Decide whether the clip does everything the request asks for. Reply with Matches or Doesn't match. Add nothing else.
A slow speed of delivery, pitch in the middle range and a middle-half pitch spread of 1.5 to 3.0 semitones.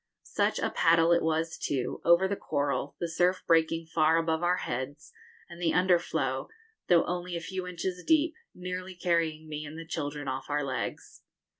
Doesn't match